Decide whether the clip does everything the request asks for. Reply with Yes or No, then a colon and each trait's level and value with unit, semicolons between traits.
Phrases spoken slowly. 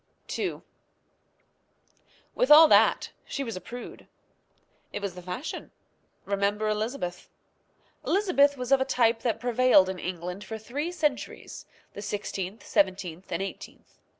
Yes: slow, 130 wpm